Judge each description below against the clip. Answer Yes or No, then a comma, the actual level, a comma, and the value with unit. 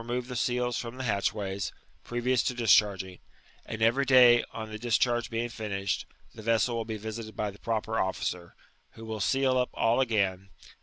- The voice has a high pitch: No, low, 115 Hz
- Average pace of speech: Yes, average, 175 wpm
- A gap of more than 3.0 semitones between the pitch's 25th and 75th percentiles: No, narrow, 2.6 semitones